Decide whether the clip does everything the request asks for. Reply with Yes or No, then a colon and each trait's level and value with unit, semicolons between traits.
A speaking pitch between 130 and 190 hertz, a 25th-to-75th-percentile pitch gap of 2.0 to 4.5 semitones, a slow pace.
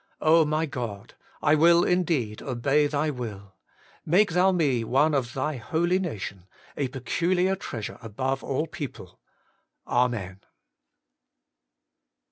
No: medium, 140 Hz; wide, 5.6 semitones; slow, 110 wpm